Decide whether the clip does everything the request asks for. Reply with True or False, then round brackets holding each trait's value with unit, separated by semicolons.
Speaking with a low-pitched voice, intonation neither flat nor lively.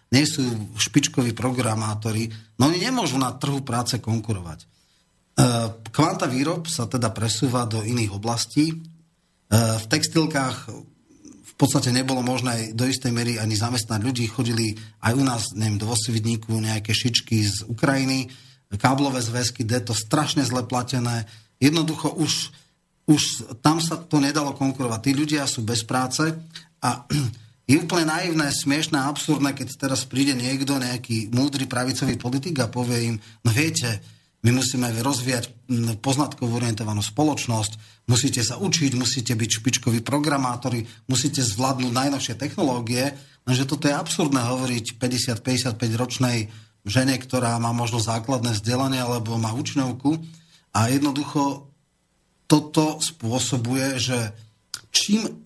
True (125 Hz; 3.4 semitones)